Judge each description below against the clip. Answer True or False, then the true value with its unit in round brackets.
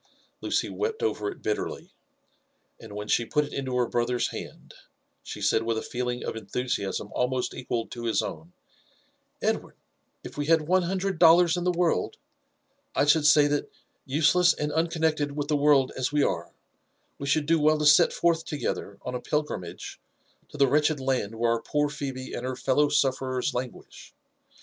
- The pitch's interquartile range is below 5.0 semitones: True (4.0 semitones)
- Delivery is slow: False (195 wpm)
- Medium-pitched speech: True (145 Hz)